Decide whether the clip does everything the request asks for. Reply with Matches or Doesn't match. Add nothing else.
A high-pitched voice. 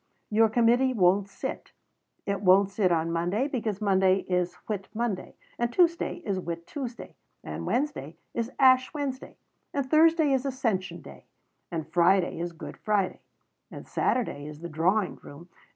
Matches